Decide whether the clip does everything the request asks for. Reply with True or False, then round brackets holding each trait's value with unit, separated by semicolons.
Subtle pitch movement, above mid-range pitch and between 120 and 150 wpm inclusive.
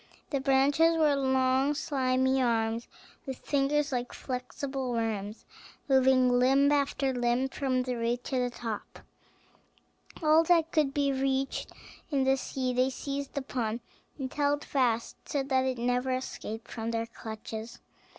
True (2.2 semitones; 260 Hz; 140 wpm)